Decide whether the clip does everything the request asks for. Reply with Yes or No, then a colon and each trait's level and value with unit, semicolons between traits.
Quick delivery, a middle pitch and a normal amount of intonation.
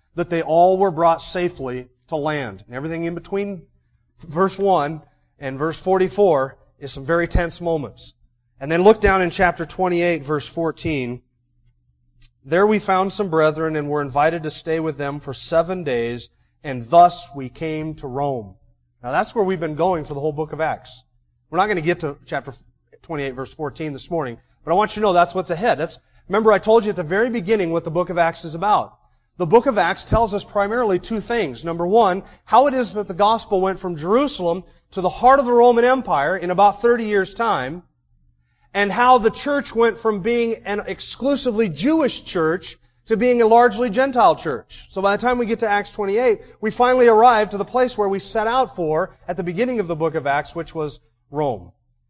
No: fast, 210 wpm; medium, 175 Hz; wide, 6.0 semitones